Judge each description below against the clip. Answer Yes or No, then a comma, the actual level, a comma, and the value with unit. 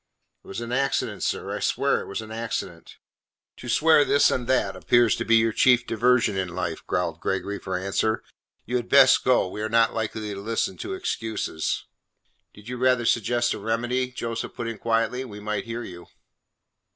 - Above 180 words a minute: Yes, average, 190 wpm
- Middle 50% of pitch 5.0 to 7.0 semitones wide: No, average, 2.9 semitones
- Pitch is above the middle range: No, low, 115 Hz